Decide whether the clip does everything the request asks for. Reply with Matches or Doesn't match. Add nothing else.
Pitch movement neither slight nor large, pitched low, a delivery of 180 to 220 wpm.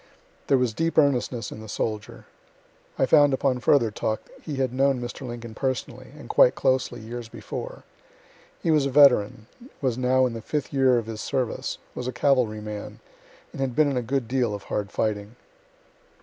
Matches